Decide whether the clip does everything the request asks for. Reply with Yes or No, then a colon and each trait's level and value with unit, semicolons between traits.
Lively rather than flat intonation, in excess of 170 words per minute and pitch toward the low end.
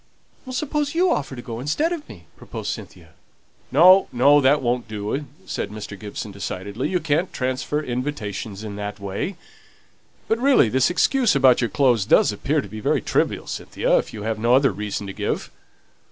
Yes: wide, 6.4 semitones; average, 180 wpm; low, 125 Hz